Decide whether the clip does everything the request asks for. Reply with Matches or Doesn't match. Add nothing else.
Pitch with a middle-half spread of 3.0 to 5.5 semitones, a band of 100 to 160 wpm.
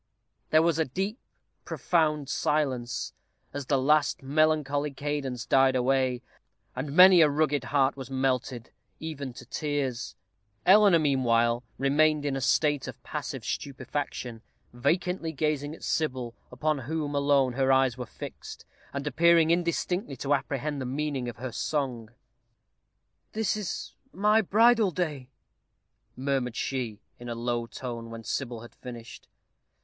Matches